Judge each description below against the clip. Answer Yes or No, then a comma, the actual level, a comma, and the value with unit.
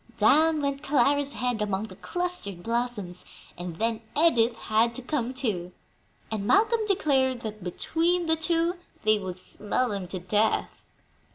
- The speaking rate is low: No, average, 150 wpm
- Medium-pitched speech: No, high, 235 Hz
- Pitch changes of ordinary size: No, wide, 6.5 semitones